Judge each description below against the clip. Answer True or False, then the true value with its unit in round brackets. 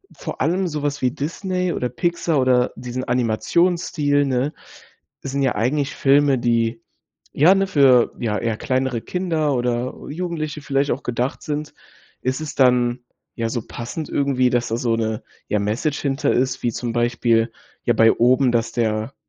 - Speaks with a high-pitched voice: False (130 Hz)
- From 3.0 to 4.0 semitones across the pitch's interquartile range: True (3.6 semitones)